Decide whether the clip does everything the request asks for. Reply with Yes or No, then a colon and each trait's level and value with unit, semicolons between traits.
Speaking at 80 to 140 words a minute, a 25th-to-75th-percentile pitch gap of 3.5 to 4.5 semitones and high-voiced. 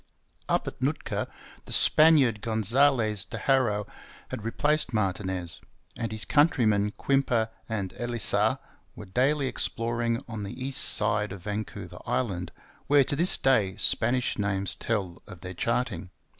No: slow, 135 wpm; average, 4.2 semitones; low, 110 Hz